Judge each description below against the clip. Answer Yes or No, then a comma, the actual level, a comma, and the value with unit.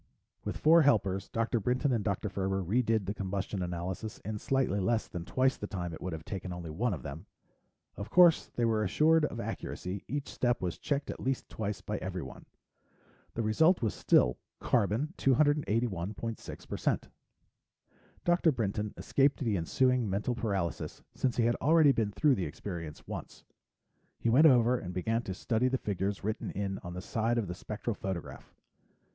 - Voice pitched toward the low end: Yes, low, 110 Hz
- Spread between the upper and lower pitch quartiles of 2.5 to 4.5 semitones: No, average, 5.0 semitones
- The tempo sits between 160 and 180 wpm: Yes, average, 170 wpm